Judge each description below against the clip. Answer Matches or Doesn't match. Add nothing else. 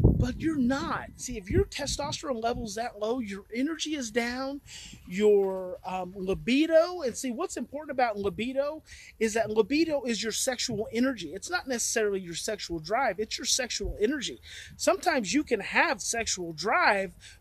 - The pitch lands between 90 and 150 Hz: Doesn't match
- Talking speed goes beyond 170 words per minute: Doesn't match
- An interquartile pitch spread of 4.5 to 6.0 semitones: Matches